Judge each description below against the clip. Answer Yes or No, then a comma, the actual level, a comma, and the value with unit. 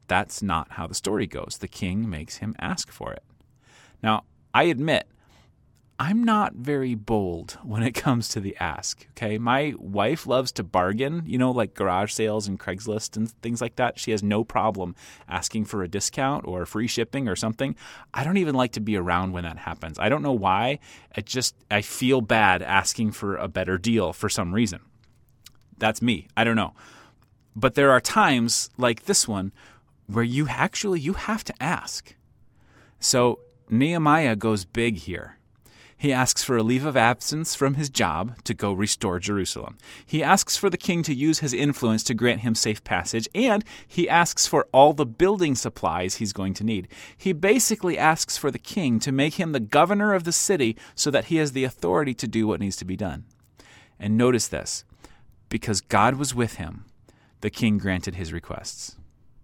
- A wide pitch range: No, average, 4.4 semitones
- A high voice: No, low, 115 Hz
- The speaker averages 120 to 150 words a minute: No, average, 190 wpm